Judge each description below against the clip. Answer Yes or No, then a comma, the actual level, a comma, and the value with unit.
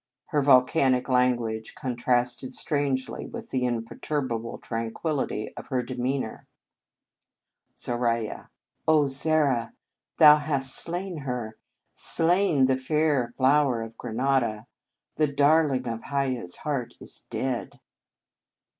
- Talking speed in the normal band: No, slow, 110 wpm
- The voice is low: Yes, low, 130 Hz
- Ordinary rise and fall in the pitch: Yes, average, 3.4 semitones